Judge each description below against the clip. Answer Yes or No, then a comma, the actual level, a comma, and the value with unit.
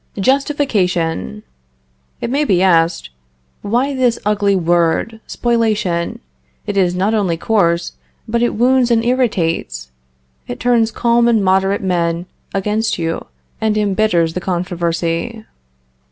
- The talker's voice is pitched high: Yes, high, 200 Hz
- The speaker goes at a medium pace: No, slow, 120 wpm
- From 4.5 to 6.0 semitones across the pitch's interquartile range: Yes, average, 5.2 semitones